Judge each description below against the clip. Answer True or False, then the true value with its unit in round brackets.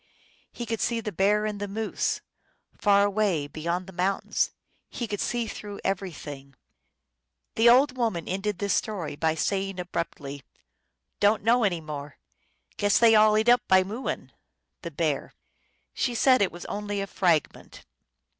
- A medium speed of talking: True (170 wpm)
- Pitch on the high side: True (200 Hz)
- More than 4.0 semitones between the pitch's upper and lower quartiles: False (3.7 semitones)